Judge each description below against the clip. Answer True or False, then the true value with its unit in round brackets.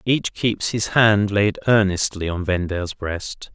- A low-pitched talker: True (100 Hz)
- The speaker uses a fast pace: False (150 wpm)